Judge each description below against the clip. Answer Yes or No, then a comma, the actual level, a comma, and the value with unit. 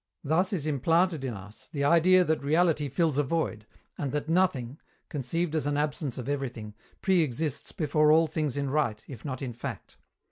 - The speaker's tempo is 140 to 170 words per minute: No, average, 185 wpm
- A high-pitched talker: No, medium, 150 Hz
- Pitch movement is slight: No, average, 3.5 semitones